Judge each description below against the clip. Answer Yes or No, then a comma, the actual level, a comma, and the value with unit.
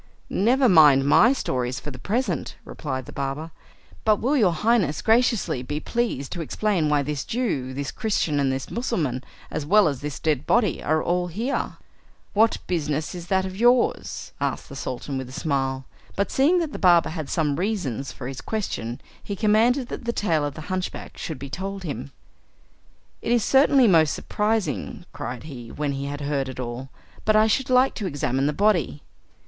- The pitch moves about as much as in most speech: No, wide, 7.7 semitones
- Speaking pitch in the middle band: Yes, medium, 160 Hz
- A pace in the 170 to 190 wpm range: Yes, average, 185 wpm